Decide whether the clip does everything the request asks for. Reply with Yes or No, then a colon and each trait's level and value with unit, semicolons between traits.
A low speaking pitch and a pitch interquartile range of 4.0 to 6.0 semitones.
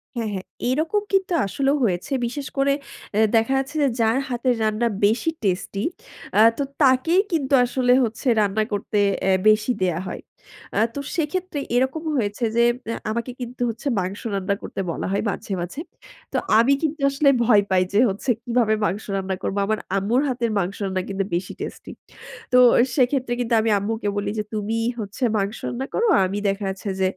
No: high, 225 Hz; average, 4.7 semitones